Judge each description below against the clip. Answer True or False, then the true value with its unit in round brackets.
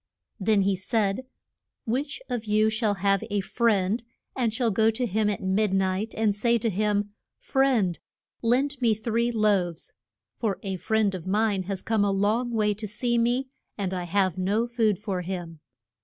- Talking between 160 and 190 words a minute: True (180 wpm)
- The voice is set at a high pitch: True (210 Hz)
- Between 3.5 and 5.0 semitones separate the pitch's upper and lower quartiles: False (2.9 semitones)